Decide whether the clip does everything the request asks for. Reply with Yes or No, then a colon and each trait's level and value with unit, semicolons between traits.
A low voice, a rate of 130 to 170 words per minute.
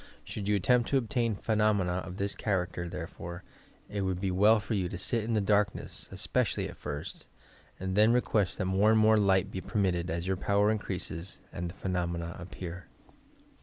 No: very low, 95 Hz; average, 190 wpm